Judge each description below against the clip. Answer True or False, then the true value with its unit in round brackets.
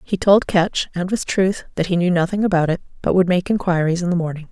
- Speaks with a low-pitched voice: False (180 Hz)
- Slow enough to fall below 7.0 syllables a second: True (5.9 syllables/s)